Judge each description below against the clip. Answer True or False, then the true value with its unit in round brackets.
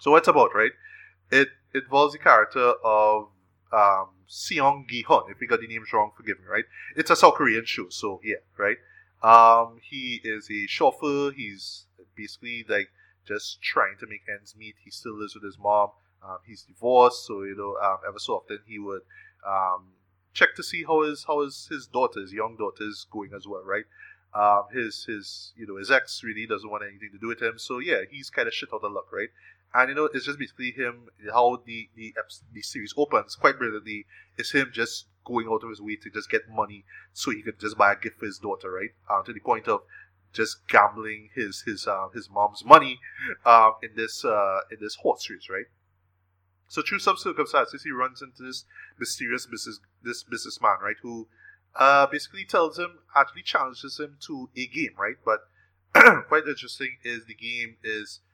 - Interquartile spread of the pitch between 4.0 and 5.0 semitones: True (4.3 semitones)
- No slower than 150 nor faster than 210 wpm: True (200 wpm)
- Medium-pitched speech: False (110 Hz)